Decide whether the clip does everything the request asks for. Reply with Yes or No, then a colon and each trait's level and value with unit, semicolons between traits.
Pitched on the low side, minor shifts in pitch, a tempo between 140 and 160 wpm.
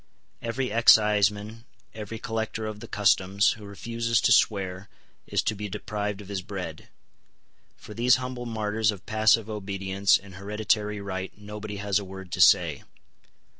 Yes: low, 105 Hz; narrow, 2.0 semitones; average, 150 wpm